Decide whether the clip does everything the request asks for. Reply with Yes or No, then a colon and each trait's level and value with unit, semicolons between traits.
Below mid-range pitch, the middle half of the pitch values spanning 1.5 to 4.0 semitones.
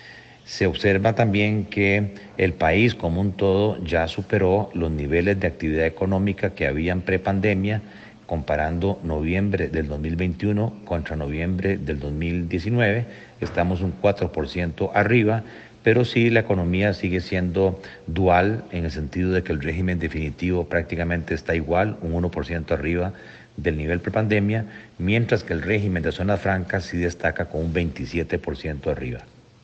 Yes: very low, 90 Hz; average, 3.5 semitones